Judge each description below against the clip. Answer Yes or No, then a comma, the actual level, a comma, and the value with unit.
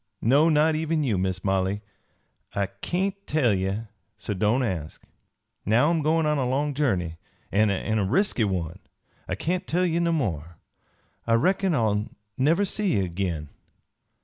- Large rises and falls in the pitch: Yes, wide, 8.8 semitones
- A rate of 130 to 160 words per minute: Yes, average, 155 wpm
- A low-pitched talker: Yes, low, 120 Hz